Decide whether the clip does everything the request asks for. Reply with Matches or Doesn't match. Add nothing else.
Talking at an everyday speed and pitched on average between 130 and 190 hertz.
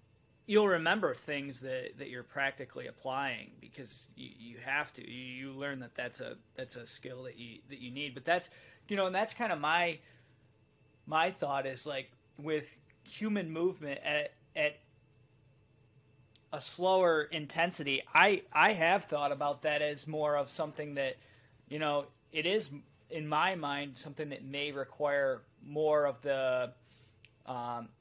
Matches